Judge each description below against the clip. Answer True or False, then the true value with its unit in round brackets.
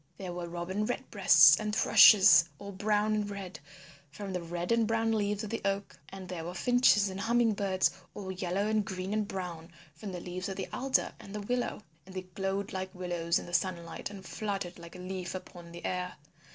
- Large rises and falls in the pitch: False (2.7 semitones)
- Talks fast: True (210 wpm)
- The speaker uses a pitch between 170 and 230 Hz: True (190 Hz)